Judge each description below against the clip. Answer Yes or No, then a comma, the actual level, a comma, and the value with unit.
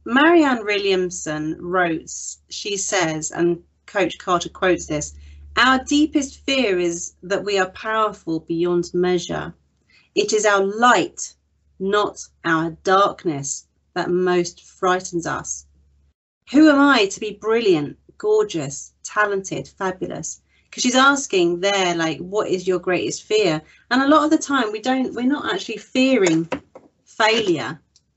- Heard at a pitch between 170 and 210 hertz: Yes, high, 190 Hz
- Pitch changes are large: Yes, wide, 6.7 semitones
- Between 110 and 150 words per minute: Yes, slow, 135 wpm